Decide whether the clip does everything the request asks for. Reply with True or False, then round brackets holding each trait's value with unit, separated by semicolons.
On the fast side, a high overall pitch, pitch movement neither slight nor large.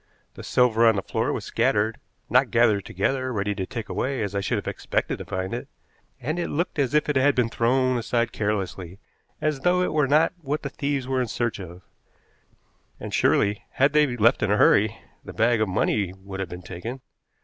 False (210 wpm; 115 Hz; 4.9 semitones)